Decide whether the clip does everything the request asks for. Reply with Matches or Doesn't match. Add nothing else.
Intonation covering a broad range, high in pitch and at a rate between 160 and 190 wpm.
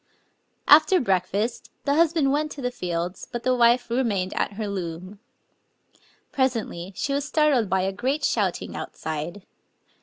Doesn't match